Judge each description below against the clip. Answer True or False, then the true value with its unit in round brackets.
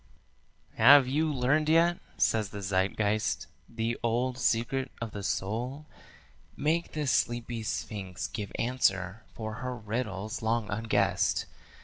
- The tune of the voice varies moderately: True (3.5 semitones)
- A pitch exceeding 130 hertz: False (115 Hz)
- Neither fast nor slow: False (120 wpm)